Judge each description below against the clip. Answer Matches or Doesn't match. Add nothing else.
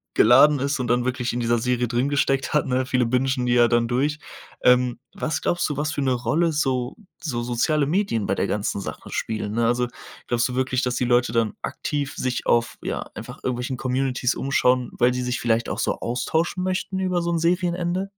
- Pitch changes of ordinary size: Matches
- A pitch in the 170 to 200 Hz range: Doesn't match